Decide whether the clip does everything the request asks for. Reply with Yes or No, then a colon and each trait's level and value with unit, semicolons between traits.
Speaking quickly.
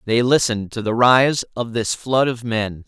Yes: fast, 210 wpm